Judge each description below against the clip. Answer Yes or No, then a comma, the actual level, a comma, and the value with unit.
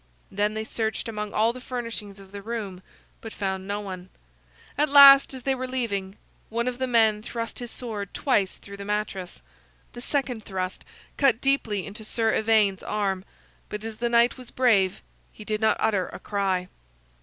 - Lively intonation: No, average, 3.2 semitones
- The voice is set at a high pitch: Yes, high, 215 Hz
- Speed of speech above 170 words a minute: Yes, average, 180 wpm